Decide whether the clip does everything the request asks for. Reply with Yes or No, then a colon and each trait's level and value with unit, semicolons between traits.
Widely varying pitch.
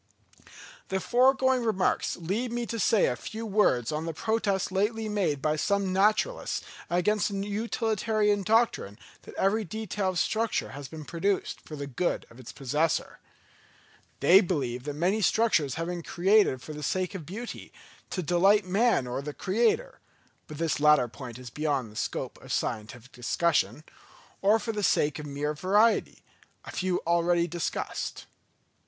Yes: wide, 6.1 semitones